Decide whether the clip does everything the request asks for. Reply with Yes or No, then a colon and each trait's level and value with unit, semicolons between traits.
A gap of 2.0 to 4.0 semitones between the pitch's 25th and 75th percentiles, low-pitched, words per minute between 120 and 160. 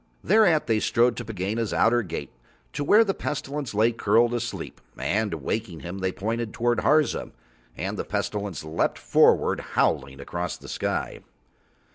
Yes: average, 3.7 semitones; low, 115 Hz; average, 155 wpm